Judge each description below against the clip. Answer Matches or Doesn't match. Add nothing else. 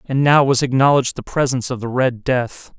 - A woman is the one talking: Doesn't match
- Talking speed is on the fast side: Matches